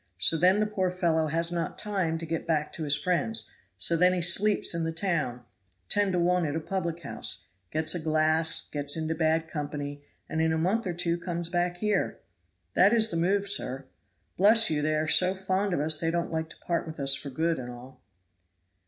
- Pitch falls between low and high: Yes, medium, 165 Hz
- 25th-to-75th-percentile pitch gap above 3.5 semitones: No, narrow, 2.6 semitones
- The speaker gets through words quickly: Yes, fast, 215 wpm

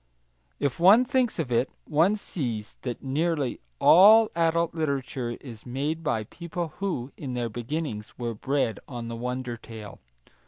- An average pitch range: No, wide, 5.9 semitones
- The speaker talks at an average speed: Yes, average, 150 wpm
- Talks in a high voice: No, medium, 140 Hz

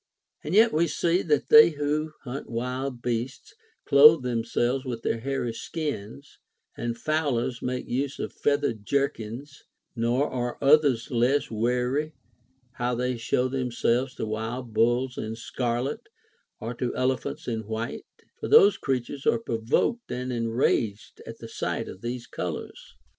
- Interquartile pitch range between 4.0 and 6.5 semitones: No, average, 3.2 semitones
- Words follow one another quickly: No, average, 140 wpm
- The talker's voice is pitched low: Yes, low, 125 Hz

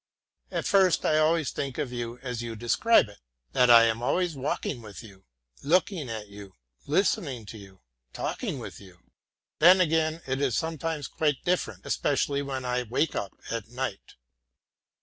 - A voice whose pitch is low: Yes, low, 130 Hz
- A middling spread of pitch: No, wide, 5.8 semitones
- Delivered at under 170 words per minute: Yes, average, 160 wpm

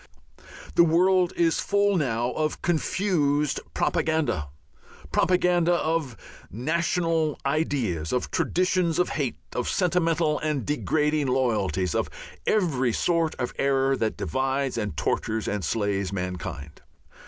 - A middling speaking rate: No, slow, 115 wpm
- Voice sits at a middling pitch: Yes, medium, 150 Hz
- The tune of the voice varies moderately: No, wide, 6.4 semitones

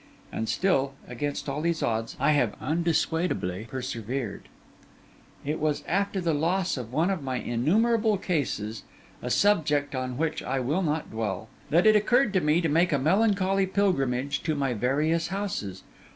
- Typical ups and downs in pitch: No, wide, 6.2 semitones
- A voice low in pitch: No, medium, 150 Hz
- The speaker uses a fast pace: No, average, 160 wpm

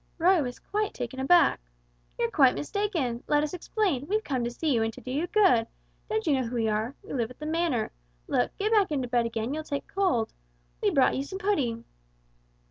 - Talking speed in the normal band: No, fast, 215 wpm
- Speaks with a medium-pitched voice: No, very high, 280 Hz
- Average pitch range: No, wide, 7.1 semitones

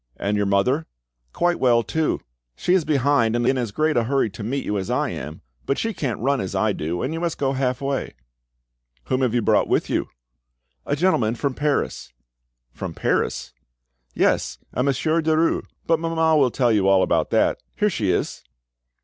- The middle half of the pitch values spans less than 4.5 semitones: No, wide, 5.6 semitones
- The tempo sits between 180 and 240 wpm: Yes, average, 190 wpm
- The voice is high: No, low, 130 Hz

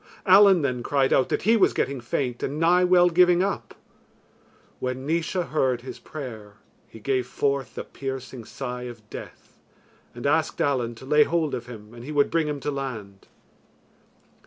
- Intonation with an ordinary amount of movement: Yes, average, 4.6 semitones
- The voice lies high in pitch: No, low, 135 Hz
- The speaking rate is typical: Yes, average, 175 wpm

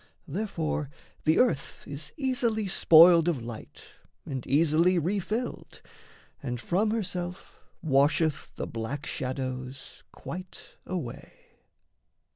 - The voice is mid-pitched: Yes, medium, 160 Hz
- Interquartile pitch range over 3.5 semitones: Yes, average, 5.2 semitones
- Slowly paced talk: Yes, slow, 95 wpm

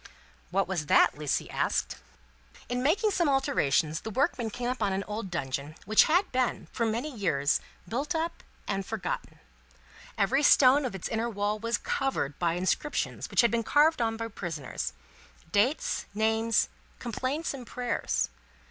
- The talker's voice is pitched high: Yes, high, 225 Hz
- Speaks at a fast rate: No, average, 150 wpm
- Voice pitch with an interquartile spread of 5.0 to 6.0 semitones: Yes, wide, 5.6 semitones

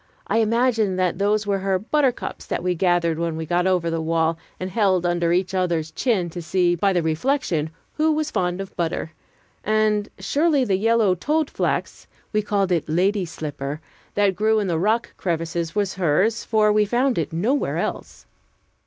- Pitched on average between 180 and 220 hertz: Yes, high, 190 Hz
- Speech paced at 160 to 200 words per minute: Yes, average, 180 wpm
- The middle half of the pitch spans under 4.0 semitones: No, average, 4.3 semitones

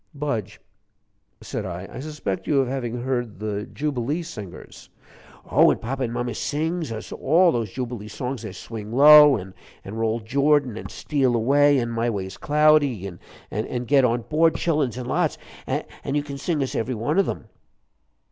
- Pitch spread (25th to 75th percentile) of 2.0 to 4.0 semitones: No, average, 4.5 semitones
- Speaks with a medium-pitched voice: No, low, 125 Hz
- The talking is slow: No, average, 170 wpm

